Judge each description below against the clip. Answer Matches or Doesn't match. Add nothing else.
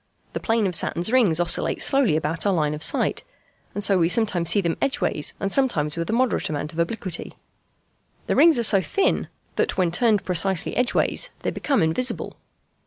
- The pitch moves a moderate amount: Doesn't match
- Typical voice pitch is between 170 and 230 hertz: Matches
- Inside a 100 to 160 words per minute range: Doesn't match